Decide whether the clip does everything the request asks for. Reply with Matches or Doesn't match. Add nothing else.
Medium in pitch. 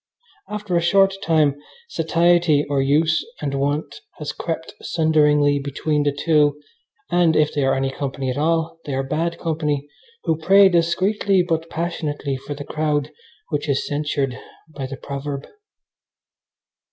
Matches